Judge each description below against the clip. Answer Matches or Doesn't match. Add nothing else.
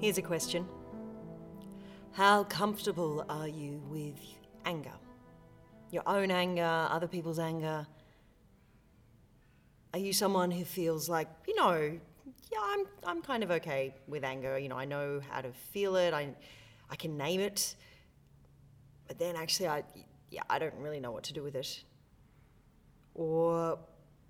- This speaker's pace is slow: Doesn't match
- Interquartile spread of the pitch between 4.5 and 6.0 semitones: Matches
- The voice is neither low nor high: Matches